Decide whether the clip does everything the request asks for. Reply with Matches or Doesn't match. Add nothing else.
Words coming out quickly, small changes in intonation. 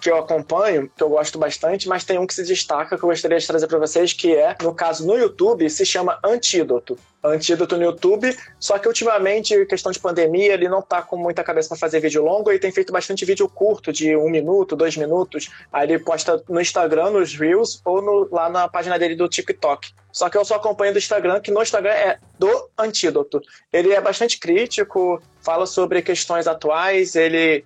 Doesn't match